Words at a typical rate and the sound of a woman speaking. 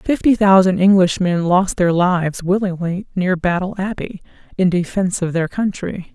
Yes: average, 145 wpm; female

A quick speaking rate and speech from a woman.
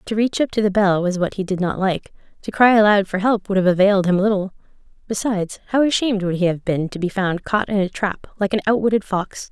Yes: fast, 250 wpm; female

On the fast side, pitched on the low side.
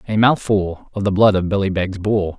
Yes: fast, 225 wpm; low, 100 Hz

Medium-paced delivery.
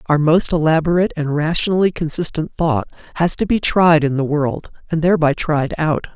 Yes: average, 175 wpm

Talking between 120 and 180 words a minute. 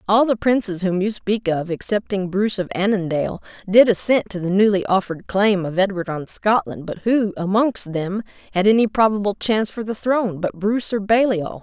No: average, 190 wpm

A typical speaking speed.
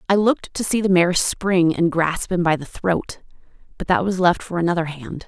No: fast, 230 wpm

